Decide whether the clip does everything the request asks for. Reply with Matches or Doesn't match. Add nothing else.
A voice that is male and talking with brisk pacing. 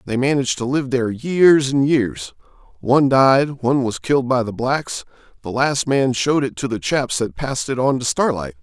Matches